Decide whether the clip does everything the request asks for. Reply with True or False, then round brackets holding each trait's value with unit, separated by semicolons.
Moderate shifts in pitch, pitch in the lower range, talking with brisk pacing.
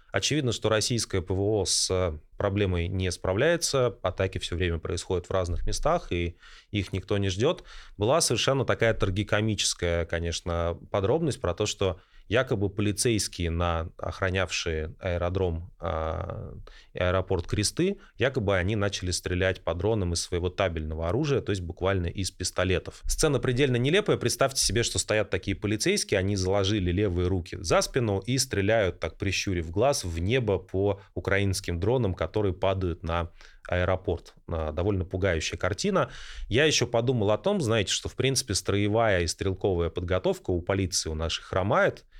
False (3.4 semitones; 95 Hz; 145 wpm)